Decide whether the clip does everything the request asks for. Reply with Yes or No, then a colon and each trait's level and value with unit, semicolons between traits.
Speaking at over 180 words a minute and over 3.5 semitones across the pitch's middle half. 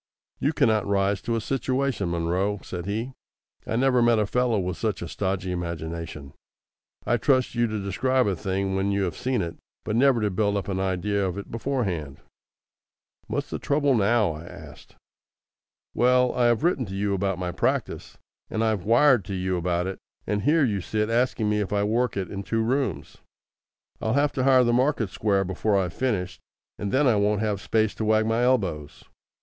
Yes: average, 195 wpm; average, 4.2 semitones